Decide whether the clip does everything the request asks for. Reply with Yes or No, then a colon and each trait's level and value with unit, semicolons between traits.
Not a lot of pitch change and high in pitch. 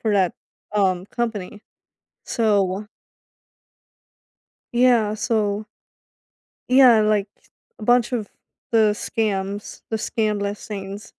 Yes: narrow, 2.0 semitones; high, 210 Hz